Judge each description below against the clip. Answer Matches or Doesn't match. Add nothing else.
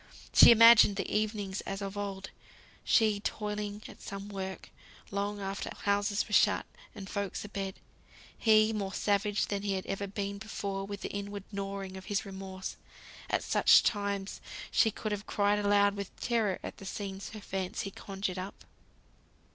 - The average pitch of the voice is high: Matches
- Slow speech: Doesn't match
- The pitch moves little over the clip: Matches